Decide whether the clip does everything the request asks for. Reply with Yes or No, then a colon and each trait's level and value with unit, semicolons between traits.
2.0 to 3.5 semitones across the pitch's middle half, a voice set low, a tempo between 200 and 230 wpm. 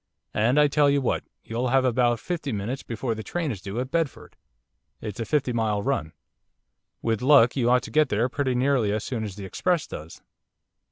No: average, 4.1 semitones; low, 125 Hz; fast, 205 wpm